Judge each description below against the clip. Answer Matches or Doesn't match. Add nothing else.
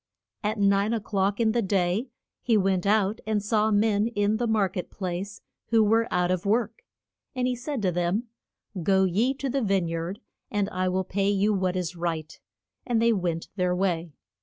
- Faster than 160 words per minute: Matches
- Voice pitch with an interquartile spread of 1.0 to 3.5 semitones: Matches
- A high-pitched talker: Matches